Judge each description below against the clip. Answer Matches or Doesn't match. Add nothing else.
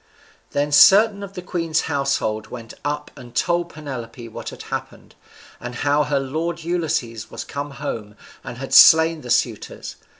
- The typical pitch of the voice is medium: Matches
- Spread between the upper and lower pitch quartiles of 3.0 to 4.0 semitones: Doesn't match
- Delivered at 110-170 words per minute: Matches